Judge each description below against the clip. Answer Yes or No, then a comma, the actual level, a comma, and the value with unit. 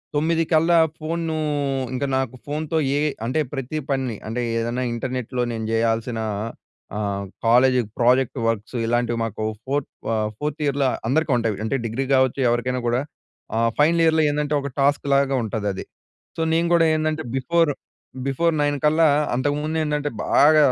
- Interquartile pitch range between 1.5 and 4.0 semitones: No, average, 4.4 semitones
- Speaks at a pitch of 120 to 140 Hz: Yes, low, 135 Hz